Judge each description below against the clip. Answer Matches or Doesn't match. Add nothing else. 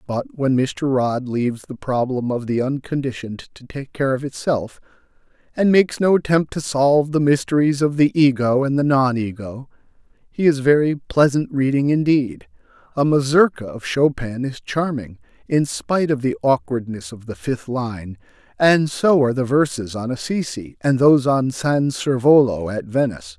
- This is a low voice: Matches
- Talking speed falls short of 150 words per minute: Doesn't match